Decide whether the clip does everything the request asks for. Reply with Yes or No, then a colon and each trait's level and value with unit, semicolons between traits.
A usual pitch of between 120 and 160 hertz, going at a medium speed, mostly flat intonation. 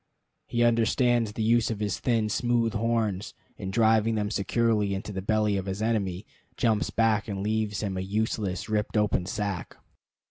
No: low, 110 Hz; average, 170 wpm; narrow, 2.1 semitones